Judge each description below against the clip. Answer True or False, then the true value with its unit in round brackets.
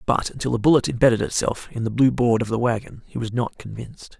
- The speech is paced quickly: True (245 wpm)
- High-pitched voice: False (120 Hz)